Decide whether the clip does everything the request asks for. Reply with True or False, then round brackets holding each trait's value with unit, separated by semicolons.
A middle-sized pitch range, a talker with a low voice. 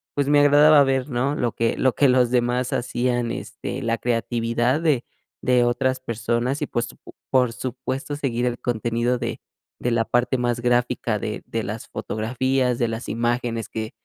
False (1.8 semitones; 125 Hz)